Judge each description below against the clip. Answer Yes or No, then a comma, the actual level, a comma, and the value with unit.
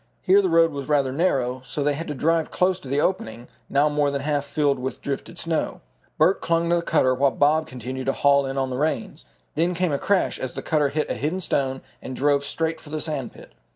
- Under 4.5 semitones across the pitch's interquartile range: Yes, average, 3.4 semitones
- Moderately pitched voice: Yes, medium, 145 Hz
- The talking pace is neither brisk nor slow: No, fast, 240 wpm